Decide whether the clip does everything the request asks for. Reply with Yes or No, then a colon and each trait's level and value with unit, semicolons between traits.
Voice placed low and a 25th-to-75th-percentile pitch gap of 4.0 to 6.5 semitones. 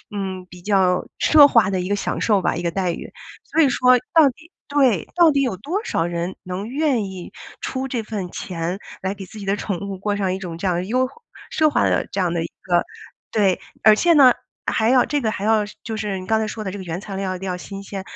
No: high, 200 Hz; average, 5.0 semitones